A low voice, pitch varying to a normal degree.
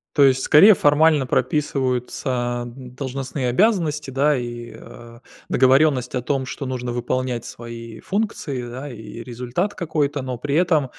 Yes: low, 130 Hz; average, 3.3 semitones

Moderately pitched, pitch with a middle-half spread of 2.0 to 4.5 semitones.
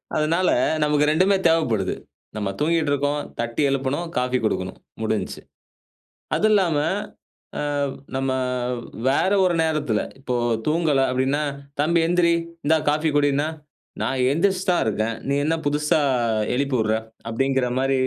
Yes: medium, 145 Hz; average, 3.8 semitones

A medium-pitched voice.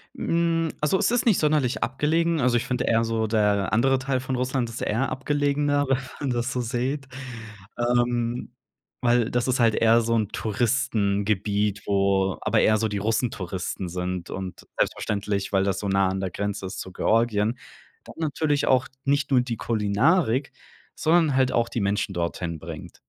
No: low, 115 Hz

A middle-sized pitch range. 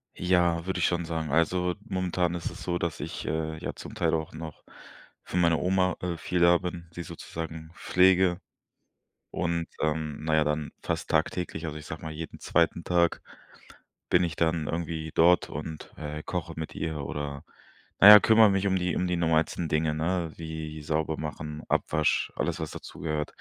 No: narrow, 2.0 semitones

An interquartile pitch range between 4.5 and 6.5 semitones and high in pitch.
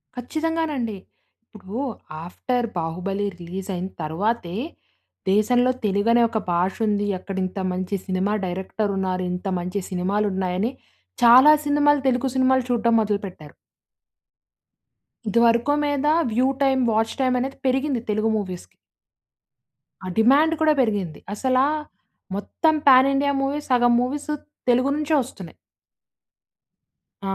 Yes: average, 5.3 semitones; high, 230 Hz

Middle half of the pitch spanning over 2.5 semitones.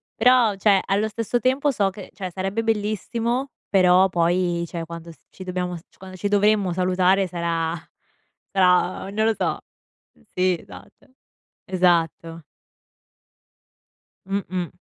Yes: average, 2.9 semitones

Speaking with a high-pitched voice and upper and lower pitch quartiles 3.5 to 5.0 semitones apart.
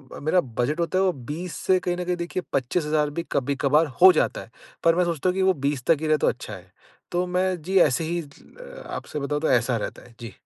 No: medium, 160 Hz; average, 4.2 semitones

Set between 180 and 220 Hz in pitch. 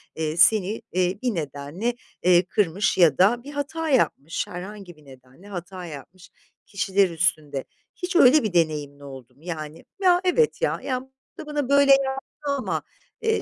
Yes: medium, 185 Hz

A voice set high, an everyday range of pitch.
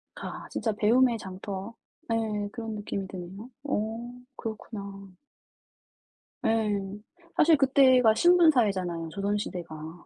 Yes: high, 215 Hz; average, 3.5 semitones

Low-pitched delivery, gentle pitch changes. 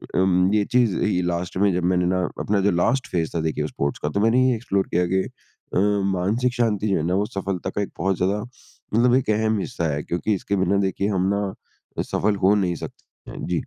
No: very low, 95 Hz; average, 3.0 semitones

